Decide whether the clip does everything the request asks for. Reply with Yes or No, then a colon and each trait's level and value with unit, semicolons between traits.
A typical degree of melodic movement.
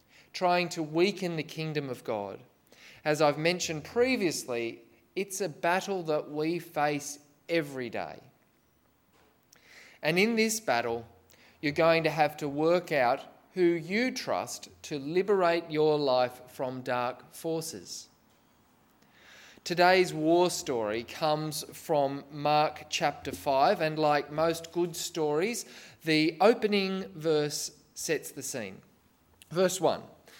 Yes: average, 3.2 semitones